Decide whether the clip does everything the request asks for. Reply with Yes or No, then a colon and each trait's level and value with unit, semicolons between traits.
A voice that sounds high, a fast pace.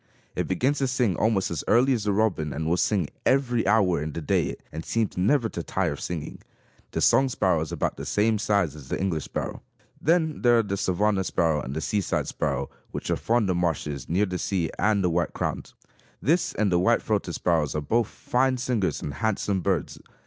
No: very low, 95 Hz; fast, 215 wpm